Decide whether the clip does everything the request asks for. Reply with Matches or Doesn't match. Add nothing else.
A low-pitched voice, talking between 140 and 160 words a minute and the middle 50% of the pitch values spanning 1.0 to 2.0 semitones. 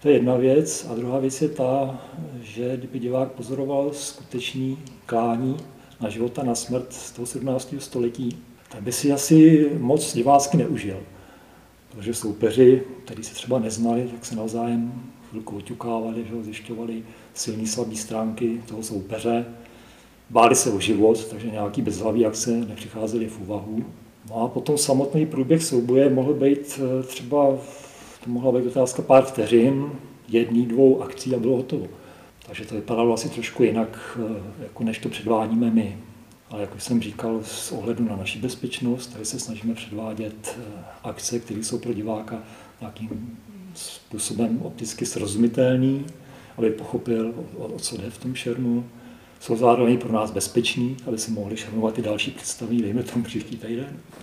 Doesn't match